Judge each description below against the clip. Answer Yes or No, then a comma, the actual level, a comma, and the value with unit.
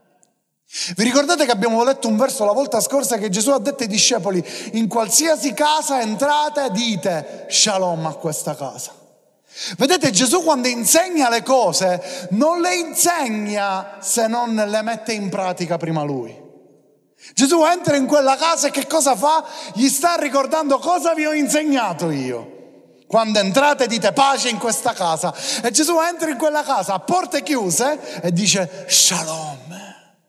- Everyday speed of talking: Yes, average, 155 wpm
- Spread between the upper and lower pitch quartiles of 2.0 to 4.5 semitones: No, wide, 7.1 semitones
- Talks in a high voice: Yes, high, 240 Hz